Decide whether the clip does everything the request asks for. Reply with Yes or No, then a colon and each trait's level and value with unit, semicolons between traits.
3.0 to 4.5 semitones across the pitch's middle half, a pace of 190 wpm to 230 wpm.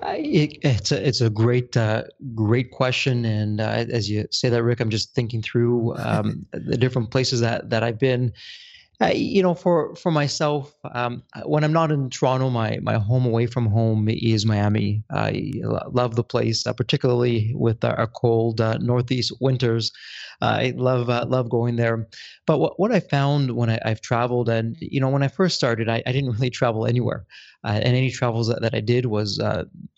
No: narrow, 2.4 semitones; average, 200 wpm